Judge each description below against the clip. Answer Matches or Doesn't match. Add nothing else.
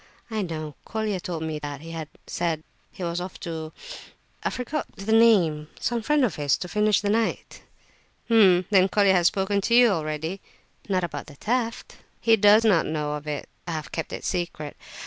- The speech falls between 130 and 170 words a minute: Doesn't match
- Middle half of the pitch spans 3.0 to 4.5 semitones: Doesn't match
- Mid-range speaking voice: Matches